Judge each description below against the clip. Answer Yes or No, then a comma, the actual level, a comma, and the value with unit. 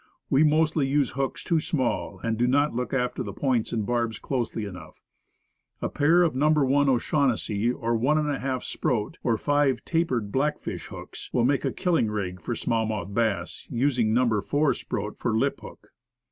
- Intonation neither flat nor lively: Yes, average, 4.4 semitones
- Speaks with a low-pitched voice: Yes, low, 125 Hz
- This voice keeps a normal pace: Yes, average, 175 wpm